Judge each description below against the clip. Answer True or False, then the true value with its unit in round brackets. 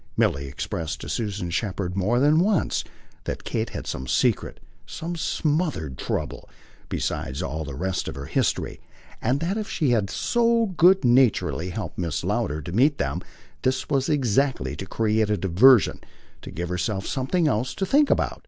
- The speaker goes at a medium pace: True (170 wpm)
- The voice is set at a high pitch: False (115 Hz)